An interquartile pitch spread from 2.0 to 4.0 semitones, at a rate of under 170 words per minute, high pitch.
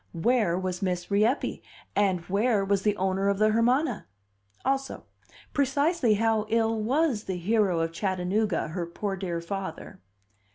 Yes: average, 3.6 semitones; average, 140 wpm; high, 205 Hz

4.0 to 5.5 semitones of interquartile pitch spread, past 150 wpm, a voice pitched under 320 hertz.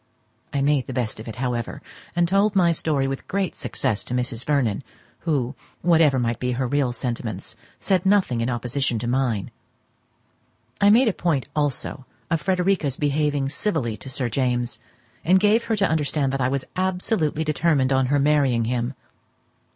Yes: average, 5.2 semitones; average, 170 wpm; medium, 140 Hz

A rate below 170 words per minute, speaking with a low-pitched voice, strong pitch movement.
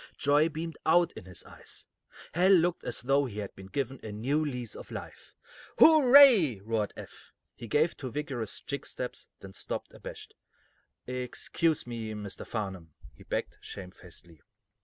Yes: average, 155 wpm; low, 125 Hz; wide, 7.0 semitones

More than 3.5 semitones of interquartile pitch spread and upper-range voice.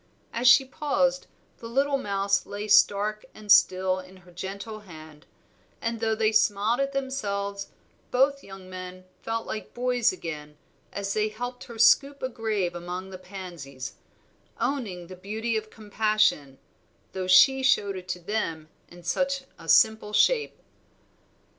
Yes: average, 4.2 semitones; high, 210 Hz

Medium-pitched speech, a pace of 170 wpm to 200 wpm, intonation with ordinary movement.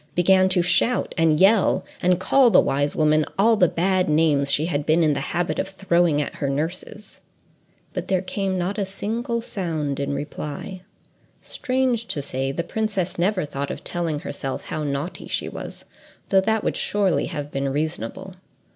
Yes: medium, 175 Hz; average, 180 wpm; average, 4.6 semitones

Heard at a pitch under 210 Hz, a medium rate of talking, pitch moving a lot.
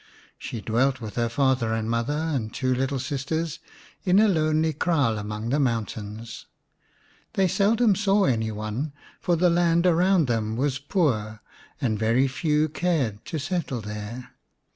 Yes: low, 135 Hz; average, 150 wpm; wide, 6.4 semitones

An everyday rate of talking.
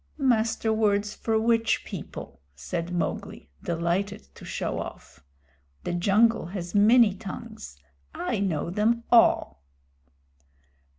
No: slow, 110 wpm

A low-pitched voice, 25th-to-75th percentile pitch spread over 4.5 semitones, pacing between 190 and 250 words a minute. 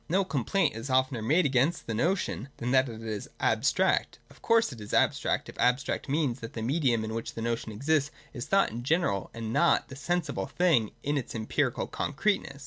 Yes: low, 130 Hz; wide, 5.5 semitones; average, 200 wpm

